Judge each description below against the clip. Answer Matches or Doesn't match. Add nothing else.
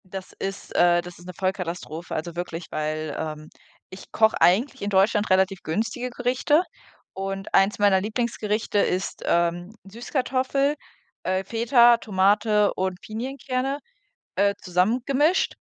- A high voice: Matches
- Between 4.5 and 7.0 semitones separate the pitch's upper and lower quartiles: Matches